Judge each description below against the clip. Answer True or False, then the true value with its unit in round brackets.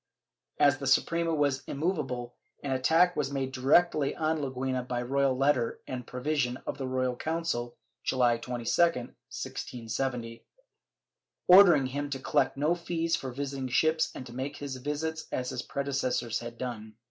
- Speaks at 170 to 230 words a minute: False (155 wpm)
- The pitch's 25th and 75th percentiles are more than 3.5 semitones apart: False (3.1 semitones)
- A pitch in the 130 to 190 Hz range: True (135 Hz)